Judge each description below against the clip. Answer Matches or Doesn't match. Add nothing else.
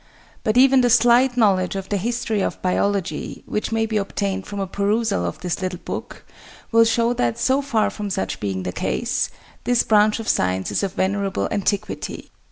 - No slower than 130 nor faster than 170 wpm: Doesn't match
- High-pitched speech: Matches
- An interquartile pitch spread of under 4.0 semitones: Matches